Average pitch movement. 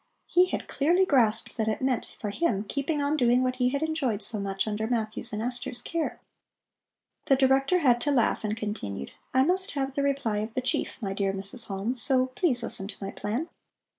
Yes: average, 4.5 semitones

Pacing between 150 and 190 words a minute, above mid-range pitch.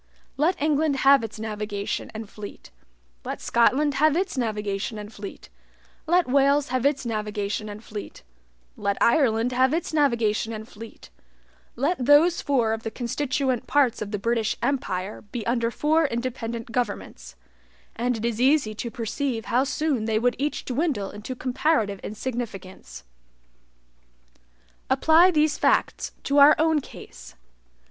No: average, 140 wpm; high, 240 Hz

